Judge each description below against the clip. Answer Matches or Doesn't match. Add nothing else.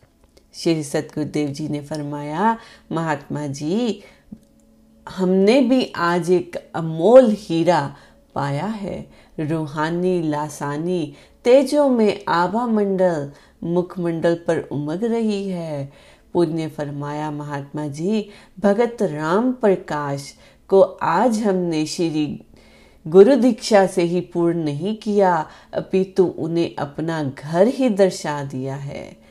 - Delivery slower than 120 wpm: Matches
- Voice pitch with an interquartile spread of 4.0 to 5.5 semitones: Matches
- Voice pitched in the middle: Matches